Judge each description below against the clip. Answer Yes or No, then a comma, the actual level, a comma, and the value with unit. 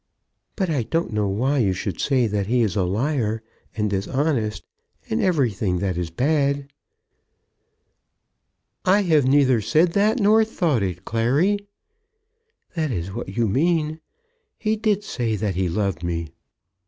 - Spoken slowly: No, average, 145 wpm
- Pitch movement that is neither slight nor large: No, wide, 8.0 semitones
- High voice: No, low, 120 Hz